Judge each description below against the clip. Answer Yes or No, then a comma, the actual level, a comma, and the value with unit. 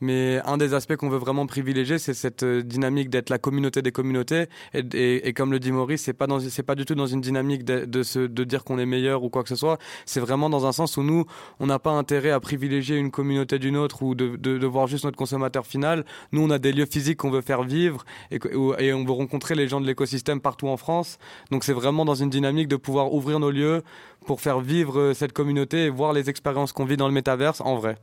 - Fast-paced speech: Yes, fast, 260 wpm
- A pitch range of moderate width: No, narrow, 1.7 semitones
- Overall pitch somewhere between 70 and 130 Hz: No, medium, 140 Hz